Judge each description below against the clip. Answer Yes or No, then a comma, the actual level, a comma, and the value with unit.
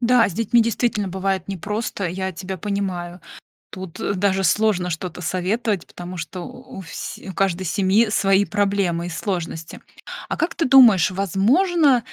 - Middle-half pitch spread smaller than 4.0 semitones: Yes, average, 3.0 semitones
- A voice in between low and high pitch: No, high, 195 Hz